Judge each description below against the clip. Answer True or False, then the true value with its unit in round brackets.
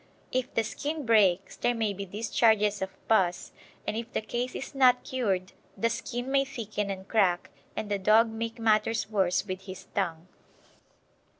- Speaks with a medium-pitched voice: False (215 Hz)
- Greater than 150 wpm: True (170 wpm)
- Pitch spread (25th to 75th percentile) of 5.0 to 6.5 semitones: False (3.2 semitones)